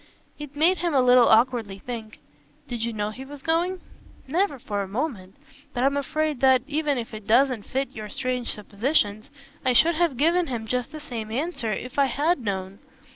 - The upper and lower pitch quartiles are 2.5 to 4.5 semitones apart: No, average, 5.0 semitones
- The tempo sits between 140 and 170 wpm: No, average, 190 wpm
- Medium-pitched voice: No, very high, 255 Hz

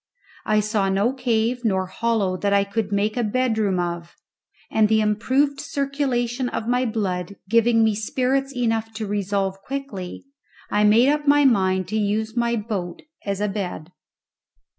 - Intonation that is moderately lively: Yes, average, 3.4 semitones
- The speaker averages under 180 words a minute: Yes, average, 160 wpm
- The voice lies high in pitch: Yes, high, 220 Hz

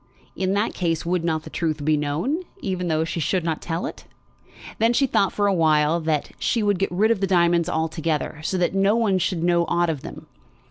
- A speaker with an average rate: No, fast, 225 wpm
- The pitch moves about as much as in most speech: Yes, average, 3.4 semitones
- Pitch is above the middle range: No, medium, 175 Hz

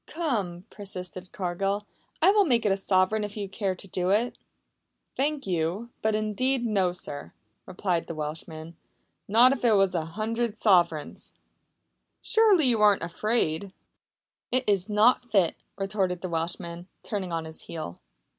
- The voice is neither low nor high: No, high, 195 Hz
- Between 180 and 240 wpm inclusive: No, average, 155 wpm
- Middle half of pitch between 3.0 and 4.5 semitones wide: Yes, average, 4.2 semitones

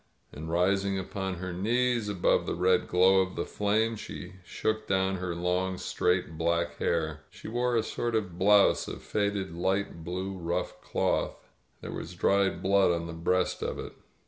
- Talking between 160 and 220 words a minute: Yes, average, 170 wpm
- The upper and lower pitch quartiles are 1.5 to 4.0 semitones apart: Yes, average, 2.7 semitones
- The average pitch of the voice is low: Yes, very low, 95 Hz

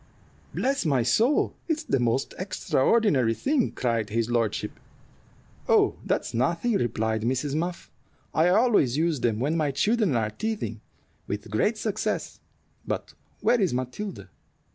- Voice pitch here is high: No, medium, 145 Hz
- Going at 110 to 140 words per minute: Yes, slow, 135 wpm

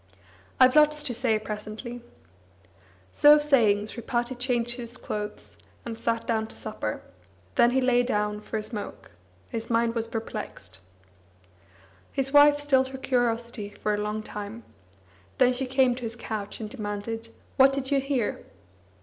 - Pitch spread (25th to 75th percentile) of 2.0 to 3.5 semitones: Yes, average, 3.2 semitones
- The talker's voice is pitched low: No, high, 235 Hz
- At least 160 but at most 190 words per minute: No, average, 150 wpm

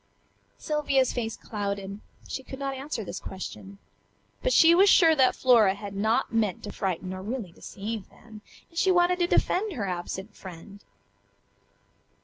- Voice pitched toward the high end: Yes, high, 220 Hz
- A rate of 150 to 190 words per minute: Yes, average, 155 wpm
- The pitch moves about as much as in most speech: No, wide, 6.1 semitones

